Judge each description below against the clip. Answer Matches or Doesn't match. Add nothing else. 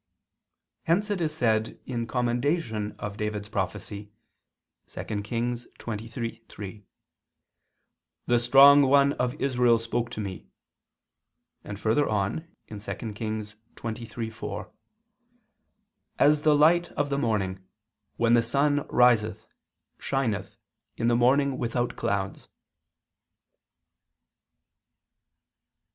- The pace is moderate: Doesn't match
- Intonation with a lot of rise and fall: Doesn't match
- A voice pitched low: Matches